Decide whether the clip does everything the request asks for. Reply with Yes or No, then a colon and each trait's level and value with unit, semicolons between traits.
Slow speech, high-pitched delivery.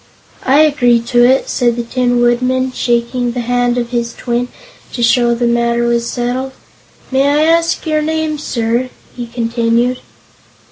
No: average, 155 wpm; high, 245 Hz